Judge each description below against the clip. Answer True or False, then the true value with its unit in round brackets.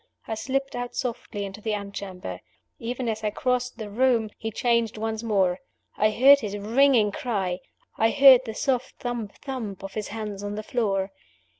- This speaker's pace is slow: False (175 wpm)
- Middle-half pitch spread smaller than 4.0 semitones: True (3.3 semitones)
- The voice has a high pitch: True (220 Hz)